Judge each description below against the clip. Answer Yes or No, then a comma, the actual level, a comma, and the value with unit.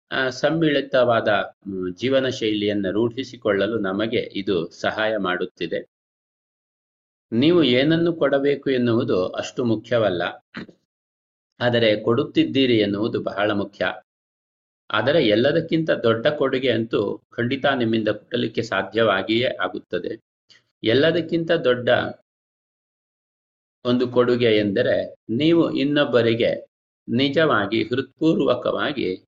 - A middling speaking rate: Yes, average, 80 wpm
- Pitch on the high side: No, low, 120 Hz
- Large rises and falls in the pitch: No, average, 4.6 semitones